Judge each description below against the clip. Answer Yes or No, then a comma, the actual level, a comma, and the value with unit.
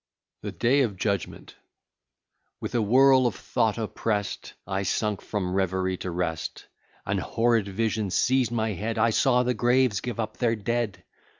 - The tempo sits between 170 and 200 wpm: No, average, 160 wpm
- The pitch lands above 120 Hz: No, low, 110 Hz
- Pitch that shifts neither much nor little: Yes, average, 3.4 semitones